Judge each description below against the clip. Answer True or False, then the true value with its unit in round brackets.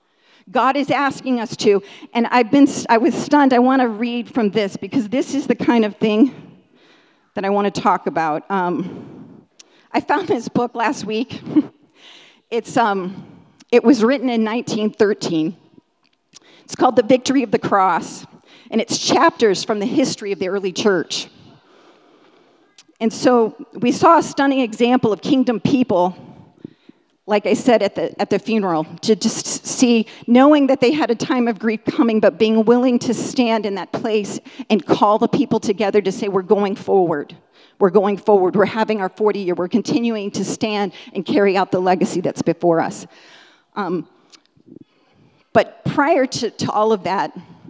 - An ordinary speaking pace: True (170 wpm)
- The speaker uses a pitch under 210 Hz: False (225 Hz)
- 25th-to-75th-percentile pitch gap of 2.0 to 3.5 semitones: False (4.6 semitones)